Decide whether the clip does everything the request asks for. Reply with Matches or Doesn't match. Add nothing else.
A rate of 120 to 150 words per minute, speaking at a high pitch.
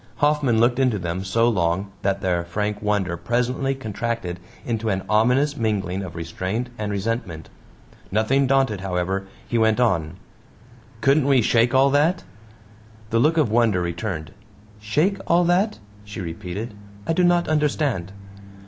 Doesn't match